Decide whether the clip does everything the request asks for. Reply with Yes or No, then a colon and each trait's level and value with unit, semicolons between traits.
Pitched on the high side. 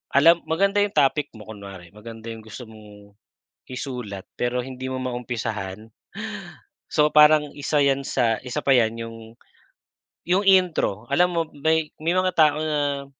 No: low, 130 Hz